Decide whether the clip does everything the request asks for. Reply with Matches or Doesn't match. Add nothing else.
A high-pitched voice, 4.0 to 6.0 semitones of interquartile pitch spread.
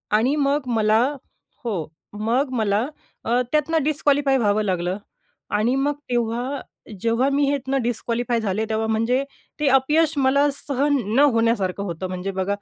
Matches